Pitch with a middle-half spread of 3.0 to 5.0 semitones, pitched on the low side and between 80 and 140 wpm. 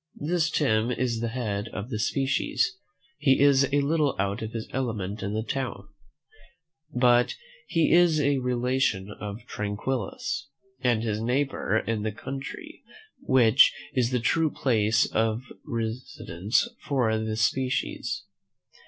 Yes: average, 3.8 semitones; low, 120 Hz; slow, 135 wpm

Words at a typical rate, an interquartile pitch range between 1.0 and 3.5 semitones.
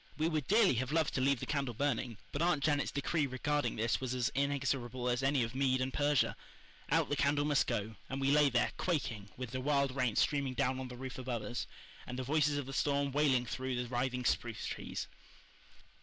No: fast, 215 wpm; narrow, 2.4 semitones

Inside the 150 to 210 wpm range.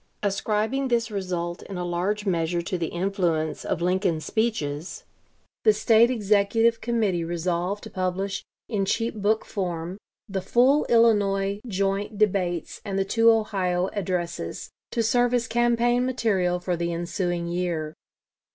No: average, 140 wpm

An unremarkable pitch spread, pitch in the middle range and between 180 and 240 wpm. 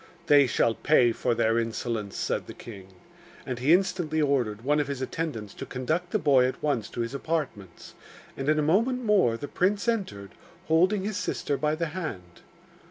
No: wide, 6.3 semitones; medium, 145 Hz; average, 185 wpm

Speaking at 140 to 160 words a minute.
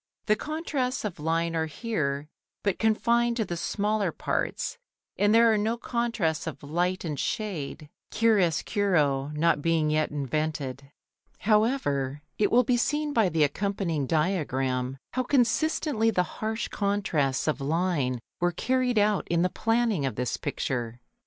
Yes: average, 145 wpm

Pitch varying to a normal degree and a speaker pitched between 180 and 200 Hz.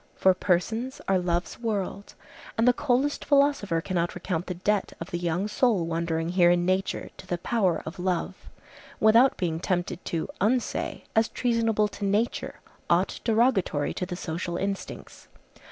Yes: average, 4.5 semitones; high, 190 Hz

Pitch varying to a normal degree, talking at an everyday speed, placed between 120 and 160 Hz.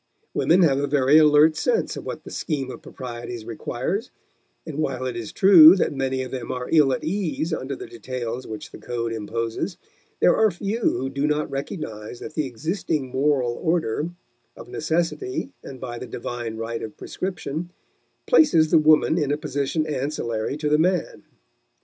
Yes: average, 4.6 semitones; average, 175 wpm; medium, 140 Hz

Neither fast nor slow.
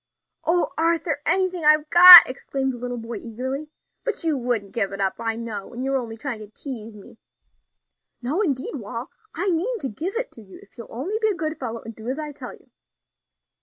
No: fast, 210 wpm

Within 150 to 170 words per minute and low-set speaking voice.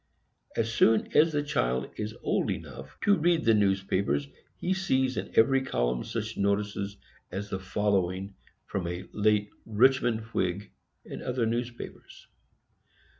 No: slow, 135 wpm; low, 105 Hz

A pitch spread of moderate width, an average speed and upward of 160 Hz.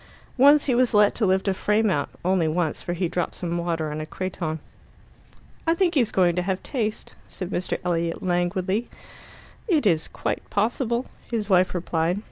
Yes: average, 4.1 semitones; average, 180 wpm; medium, 185 Hz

